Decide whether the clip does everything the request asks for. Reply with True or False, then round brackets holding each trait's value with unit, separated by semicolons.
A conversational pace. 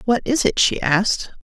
False (210 wpm)